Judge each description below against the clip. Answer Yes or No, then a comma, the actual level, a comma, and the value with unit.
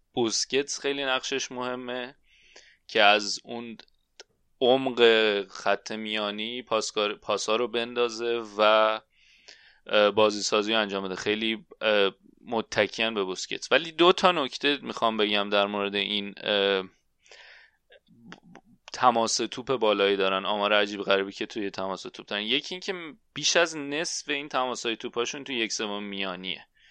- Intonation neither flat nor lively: Yes, average, 3.8 semitones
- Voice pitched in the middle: No, low, 110 Hz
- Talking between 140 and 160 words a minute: No, average, 125 wpm